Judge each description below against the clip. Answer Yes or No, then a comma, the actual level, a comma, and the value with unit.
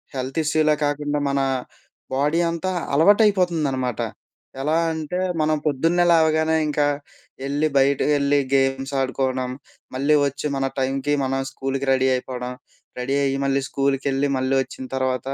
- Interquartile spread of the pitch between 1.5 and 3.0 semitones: Yes, narrow, 2.4 semitones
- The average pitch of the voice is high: No, medium, 140 Hz